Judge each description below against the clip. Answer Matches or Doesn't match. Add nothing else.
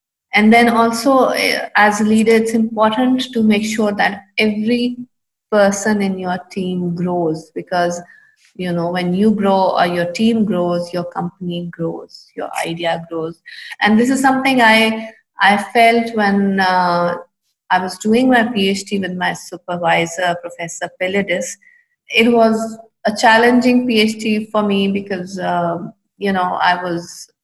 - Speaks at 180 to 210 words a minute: Doesn't match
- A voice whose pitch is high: Matches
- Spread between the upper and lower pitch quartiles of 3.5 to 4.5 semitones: Matches